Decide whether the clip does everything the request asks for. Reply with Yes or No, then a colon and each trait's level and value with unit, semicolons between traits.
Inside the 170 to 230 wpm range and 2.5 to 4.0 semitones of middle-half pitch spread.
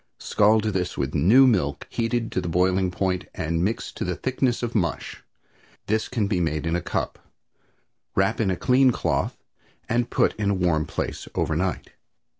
No: average, 175 wpm; average, 4.7 semitones